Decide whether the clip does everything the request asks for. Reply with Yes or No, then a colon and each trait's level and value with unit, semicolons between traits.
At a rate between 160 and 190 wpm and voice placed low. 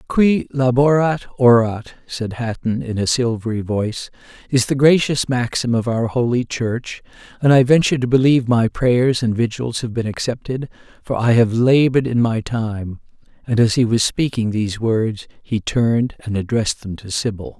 Yes: average, 170 wpm; low, 120 Hz